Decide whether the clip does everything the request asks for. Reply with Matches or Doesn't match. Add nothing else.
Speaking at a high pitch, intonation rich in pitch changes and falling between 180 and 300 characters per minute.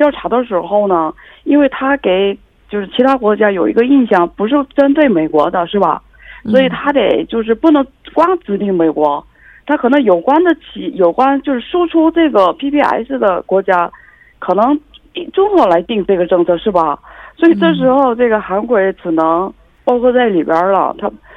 Matches